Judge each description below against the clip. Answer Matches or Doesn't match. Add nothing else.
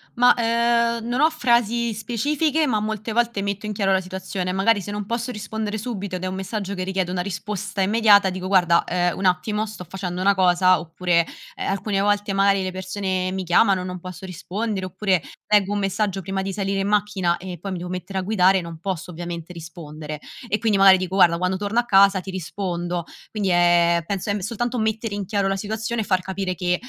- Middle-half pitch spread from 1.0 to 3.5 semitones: Matches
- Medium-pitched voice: Doesn't match